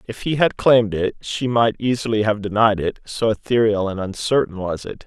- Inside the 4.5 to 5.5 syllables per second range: Yes, 5.2 syllables/s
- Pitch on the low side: Yes, low, 110 Hz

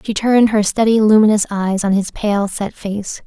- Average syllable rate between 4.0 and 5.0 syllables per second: Yes, 4.9 syllables/s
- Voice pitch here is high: Yes, high, 210 Hz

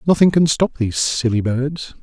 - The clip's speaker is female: No, male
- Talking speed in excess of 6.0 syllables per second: No, 5.0 syllables/s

